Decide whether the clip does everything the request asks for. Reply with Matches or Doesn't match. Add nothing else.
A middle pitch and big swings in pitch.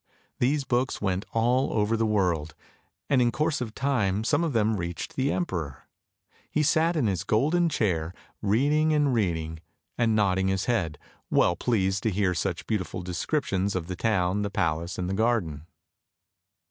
Doesn't match